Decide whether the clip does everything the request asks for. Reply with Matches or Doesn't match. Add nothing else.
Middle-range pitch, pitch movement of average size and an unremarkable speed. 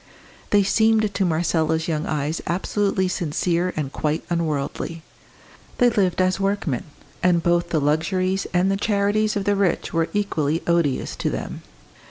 Matches